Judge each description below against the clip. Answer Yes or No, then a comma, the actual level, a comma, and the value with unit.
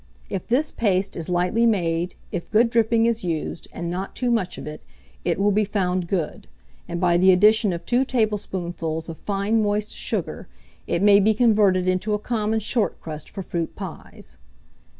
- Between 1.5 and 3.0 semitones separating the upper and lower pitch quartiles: No, average, 3.8 semitones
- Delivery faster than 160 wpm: Yes, average, 180 wpm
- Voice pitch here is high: Yes, high, 195 Hz